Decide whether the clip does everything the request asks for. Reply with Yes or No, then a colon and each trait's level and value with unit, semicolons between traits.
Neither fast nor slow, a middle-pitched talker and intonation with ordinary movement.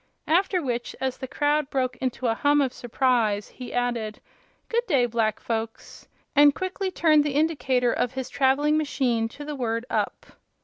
No: average, 170 wpm; very high, 260 Hz; average, 3.7 semitones